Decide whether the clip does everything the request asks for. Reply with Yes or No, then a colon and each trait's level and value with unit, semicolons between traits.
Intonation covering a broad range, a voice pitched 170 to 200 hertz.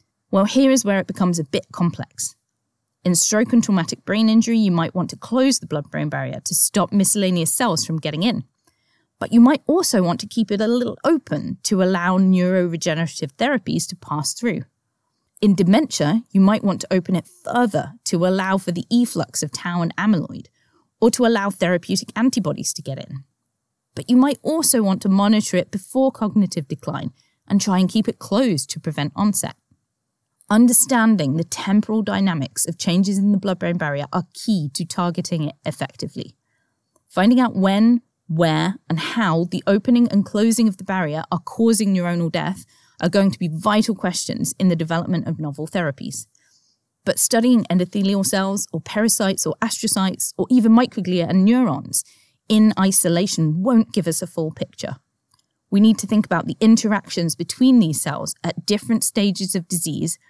No: average, 4.4 semitones; high, 190 Hz